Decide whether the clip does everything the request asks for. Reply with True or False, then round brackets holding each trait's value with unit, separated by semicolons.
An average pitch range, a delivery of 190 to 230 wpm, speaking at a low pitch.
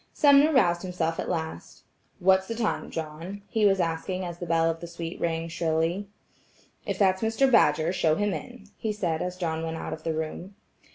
False (3.7 semitones; 195 wpm; 175 Hz)